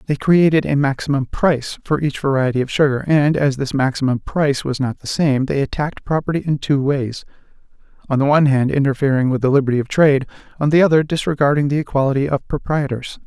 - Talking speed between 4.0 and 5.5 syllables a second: No, 6.2 syllables/s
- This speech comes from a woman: No, male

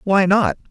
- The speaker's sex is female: Yes, female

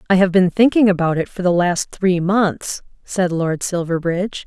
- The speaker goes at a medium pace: Yes, average, 190 wpm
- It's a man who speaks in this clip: No, female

